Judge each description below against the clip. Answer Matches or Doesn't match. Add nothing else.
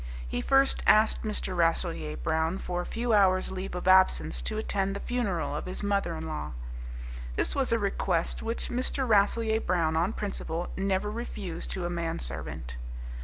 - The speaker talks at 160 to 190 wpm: Matches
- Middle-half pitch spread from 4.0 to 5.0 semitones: Matches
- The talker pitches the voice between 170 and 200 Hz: Matches